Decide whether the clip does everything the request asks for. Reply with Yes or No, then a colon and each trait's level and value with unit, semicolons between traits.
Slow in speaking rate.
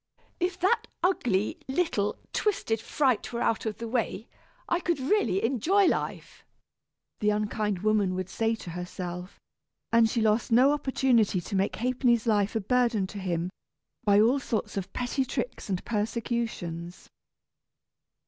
No: average, 145 wpm